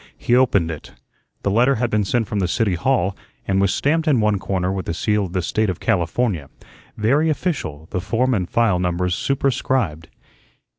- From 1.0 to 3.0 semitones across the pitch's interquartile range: No, wide, 5.4 semitones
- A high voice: No, low, 105 Hz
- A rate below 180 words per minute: No, average, 190 wpm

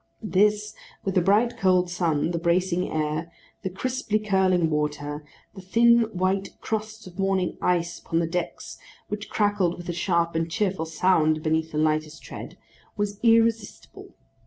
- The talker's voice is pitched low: No, medium, 185 Hz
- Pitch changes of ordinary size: Yes, average, 4.0 semitones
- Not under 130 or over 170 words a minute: Yes, average, 155 wpm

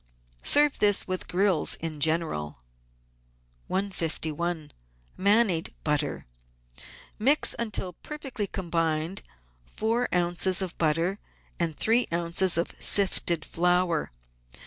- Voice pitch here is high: No, medium, 175 Hz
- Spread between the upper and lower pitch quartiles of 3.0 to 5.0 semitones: Yes, average, 3.5 semitones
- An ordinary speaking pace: No, slow, 100 wpm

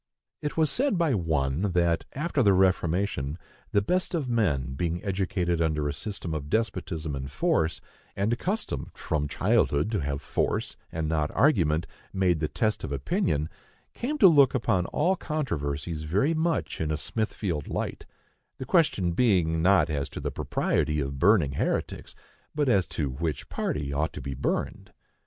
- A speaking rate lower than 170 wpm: Yes, average, 160 wpm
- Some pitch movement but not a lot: No, wide, 7.1 semitones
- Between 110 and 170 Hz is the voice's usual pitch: No, very low, 85 Hz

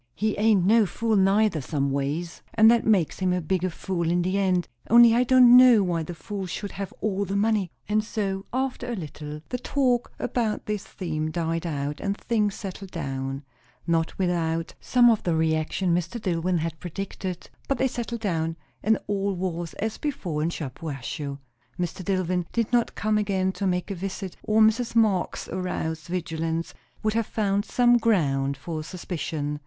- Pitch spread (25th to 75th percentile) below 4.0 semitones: No, average, 4.7 semitones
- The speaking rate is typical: Yes, average, 180 wpm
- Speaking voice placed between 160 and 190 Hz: Yes, medium, 185 Hz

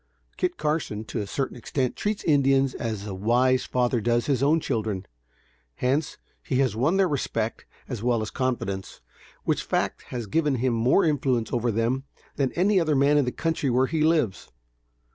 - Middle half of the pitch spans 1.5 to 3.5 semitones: No, average, 4.1 semitones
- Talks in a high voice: No, low, 130 Hz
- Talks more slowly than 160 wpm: No, average, 180 wpm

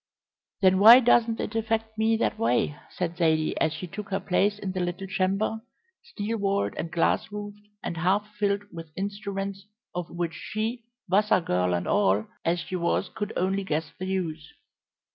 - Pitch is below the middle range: No, high, 195 Hz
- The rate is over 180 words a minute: No, average, 175 wpm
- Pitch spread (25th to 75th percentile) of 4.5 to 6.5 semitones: No, average, 3.4 semitones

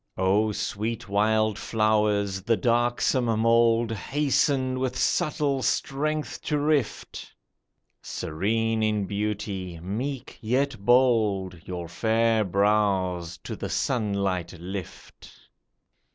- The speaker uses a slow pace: Yes, slow, 95 wpm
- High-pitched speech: No, low, 110 Hz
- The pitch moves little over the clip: No, average, 3.6 semitones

